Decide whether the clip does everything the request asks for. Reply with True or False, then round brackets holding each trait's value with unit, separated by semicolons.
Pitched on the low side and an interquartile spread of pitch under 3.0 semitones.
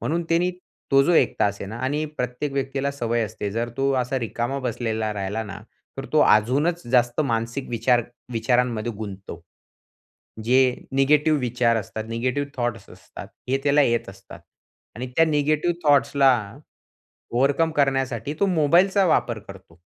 False (125 Hz; 3.8 semitones)